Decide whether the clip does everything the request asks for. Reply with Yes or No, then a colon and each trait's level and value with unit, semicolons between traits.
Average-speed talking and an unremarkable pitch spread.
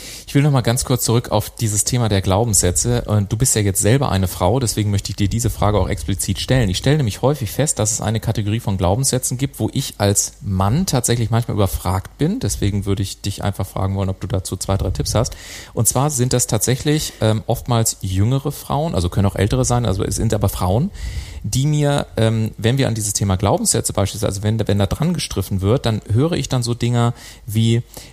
No: fast, 220 wpm; average, 3.8 semitones